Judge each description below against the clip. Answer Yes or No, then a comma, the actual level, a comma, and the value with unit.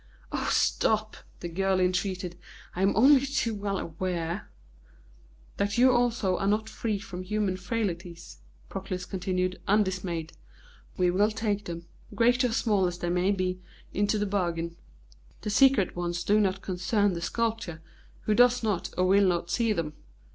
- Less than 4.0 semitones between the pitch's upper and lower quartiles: Yes, average, 3.2 semitones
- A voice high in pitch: Yes, high, 195 Hz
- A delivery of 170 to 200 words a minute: No, average, 160 wpm